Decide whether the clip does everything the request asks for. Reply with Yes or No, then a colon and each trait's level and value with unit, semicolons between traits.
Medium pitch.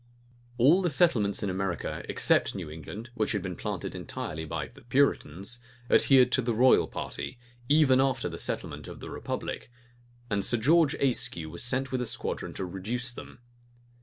No: low, 120 Hz